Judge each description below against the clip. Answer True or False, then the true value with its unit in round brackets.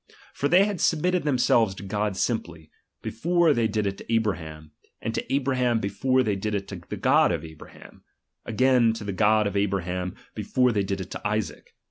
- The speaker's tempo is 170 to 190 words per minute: False (200 wpm)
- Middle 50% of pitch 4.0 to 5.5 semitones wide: True (4.6 semitones)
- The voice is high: False (110 Hz)